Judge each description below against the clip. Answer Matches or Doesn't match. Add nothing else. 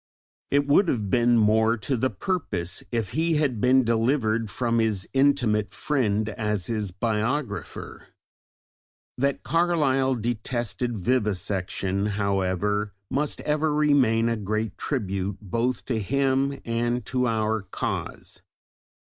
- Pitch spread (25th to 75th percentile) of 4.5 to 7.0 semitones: Doesn't match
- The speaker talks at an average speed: Doesn't match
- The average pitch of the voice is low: Matches